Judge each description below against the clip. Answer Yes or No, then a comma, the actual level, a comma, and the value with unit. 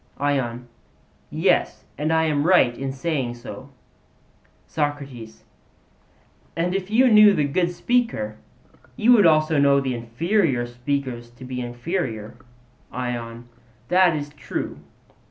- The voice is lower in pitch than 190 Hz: Yes, medium, 140 Hz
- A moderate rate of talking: No, slow, 120 wpm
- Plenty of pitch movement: Yes, wide, 5.8 semitones